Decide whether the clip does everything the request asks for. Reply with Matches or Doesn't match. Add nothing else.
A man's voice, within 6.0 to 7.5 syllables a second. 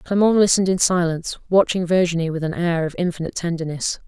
Doesn't match